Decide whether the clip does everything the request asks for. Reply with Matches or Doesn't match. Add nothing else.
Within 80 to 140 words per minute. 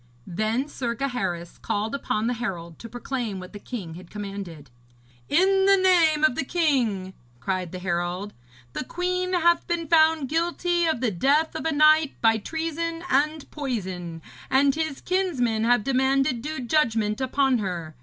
Doesn't match